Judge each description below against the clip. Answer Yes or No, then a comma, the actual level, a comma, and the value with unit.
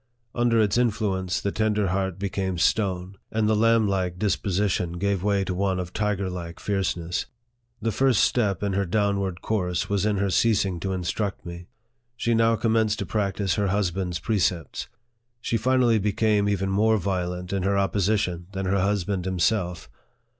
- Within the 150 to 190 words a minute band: Yes, average, 160 wpm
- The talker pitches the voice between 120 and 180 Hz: No, low, 100 Hz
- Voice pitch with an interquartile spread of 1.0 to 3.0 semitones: Yes, narrow, 2.5 semitones